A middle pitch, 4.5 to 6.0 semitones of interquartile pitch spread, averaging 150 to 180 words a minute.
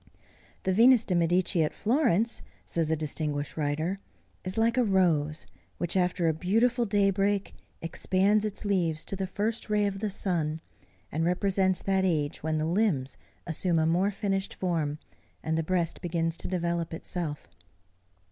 No: medium, 180 Hz; average, 3.6 semitones; average, 155 wpm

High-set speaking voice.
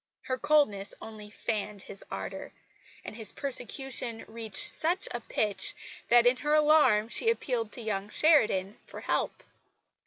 Yes: high, 230 Hz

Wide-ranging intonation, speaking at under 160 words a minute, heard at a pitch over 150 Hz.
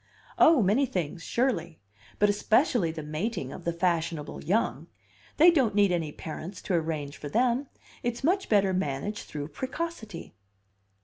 Yes: wide, 6.8 semitones; average, 145 wpm; high, 190 Hz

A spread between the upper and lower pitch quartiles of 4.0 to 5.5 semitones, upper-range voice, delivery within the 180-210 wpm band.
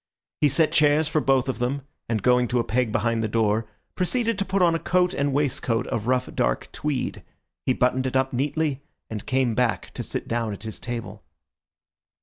No: average, 4.3 semitones; low, 130 Hz; average, 200 wpm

